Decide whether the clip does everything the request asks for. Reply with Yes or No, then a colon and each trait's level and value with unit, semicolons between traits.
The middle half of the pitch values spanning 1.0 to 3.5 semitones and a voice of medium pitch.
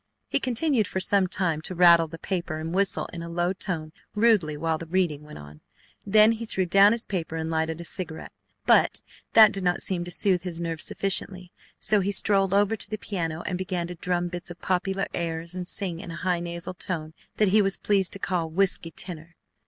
Yes: average, 2.9 semitones; medium, 180 Hz